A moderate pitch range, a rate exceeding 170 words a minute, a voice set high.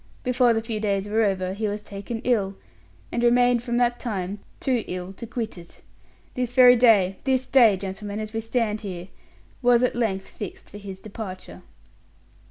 Yes: average, 3.6 semitones; average, 180 wpm; high, 220 Hz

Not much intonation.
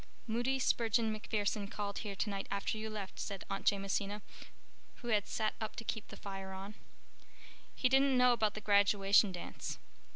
Yes: narrow, 2.1 semitones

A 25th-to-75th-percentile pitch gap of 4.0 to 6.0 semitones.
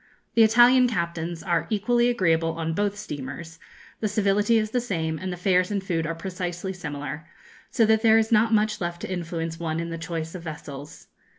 Yes: average, 4.6 semitones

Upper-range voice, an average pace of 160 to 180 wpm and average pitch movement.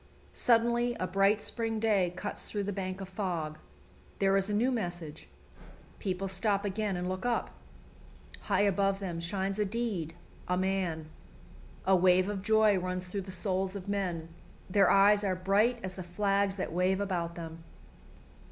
No: high, 195 Hz; average, 165 wpm; narrow, 2.0 semitones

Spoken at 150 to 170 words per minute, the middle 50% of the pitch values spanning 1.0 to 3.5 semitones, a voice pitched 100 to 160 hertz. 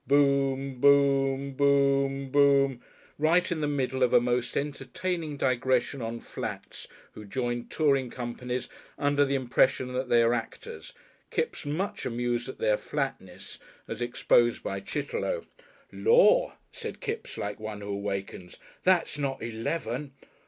No: slow, 135 wpm; average, 3.0 semitones; low, 135 Hz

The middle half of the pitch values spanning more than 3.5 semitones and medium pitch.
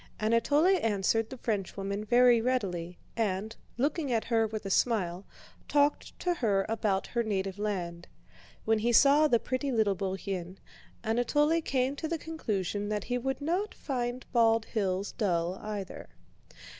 No: average, 4.6 semitones; high, 225 Hz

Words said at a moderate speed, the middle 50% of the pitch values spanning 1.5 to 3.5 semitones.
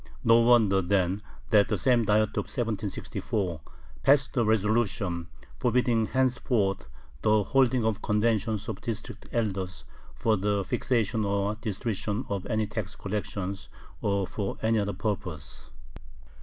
No: slow, 130 wpm; narrow, 2.6 semitones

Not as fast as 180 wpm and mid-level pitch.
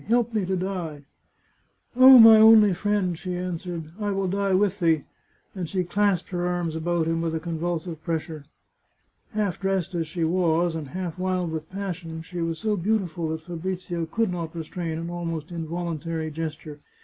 No: average, 185 wpm; medium, 175 Hz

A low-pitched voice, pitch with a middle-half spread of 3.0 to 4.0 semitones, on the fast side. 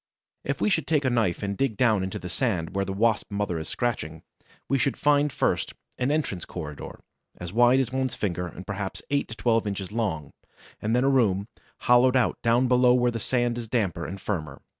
No: low, 115 Hz; average, 4.8 semitones; fast, 210 wpm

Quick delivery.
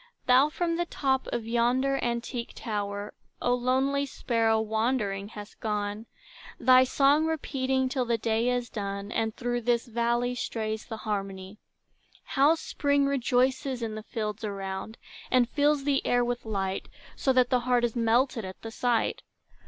No: average, 155 wpm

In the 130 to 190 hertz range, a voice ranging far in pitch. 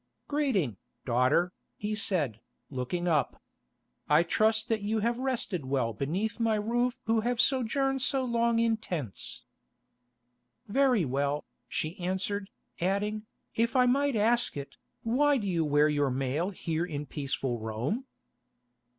No: high, 200 Hz; wide, 8.0 semitones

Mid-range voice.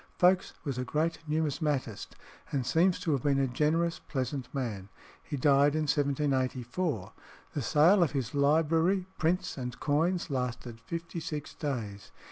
Yes: medium, 145 Hz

